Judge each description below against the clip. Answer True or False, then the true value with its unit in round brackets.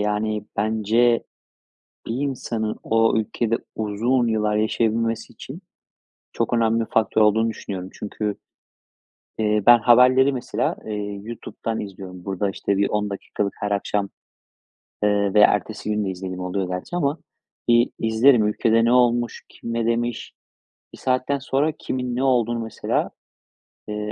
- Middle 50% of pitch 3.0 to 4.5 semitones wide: False (2.4 semitones)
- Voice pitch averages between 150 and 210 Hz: False (110 Hz)